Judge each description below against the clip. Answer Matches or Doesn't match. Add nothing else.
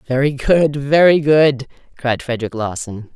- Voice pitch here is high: Doesn't match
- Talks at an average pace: Doesn't match